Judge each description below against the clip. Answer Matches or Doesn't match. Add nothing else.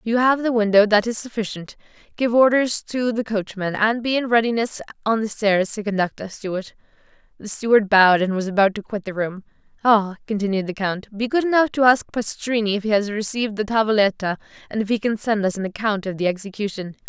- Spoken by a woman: Matches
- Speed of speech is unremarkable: Doesn't match